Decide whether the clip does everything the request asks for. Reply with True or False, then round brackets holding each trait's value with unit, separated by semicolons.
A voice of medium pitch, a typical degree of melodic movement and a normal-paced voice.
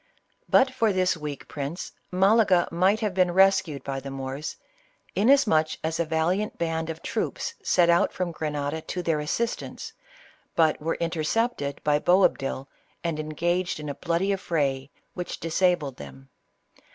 True (165 Hz; 3.8 semitones; 150 wpm)